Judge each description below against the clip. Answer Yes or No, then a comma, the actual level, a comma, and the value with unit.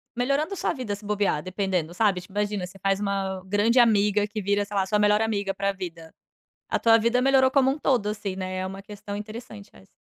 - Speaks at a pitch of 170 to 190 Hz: No, high, 205 Hz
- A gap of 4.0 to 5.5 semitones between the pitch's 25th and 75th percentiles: No, narrow, 2.5 semitones